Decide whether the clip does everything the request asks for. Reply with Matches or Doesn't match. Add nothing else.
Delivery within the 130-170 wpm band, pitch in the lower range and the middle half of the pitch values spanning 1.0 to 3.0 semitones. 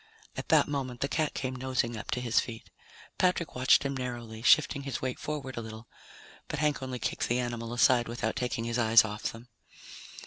Doesn't match